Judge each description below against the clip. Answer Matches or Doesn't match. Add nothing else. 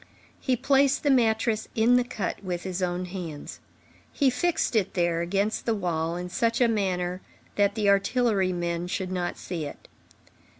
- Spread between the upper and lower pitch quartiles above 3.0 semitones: Matches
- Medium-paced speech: Matches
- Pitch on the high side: Matches